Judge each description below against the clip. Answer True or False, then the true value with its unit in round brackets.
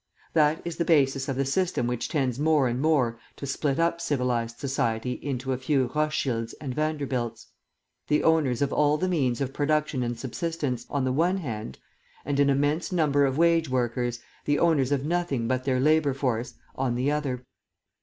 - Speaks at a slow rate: False (185 wpm)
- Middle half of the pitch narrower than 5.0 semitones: True (3.3 semitones)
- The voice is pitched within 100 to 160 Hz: True (140 Hz)